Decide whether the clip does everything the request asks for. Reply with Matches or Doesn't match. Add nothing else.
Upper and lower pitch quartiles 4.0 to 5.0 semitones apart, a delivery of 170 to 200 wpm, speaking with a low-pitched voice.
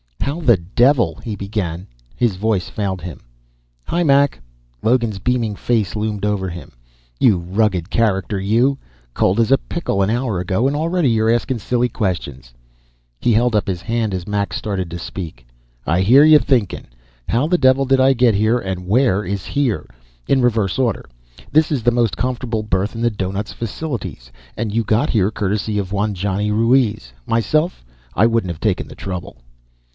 Matches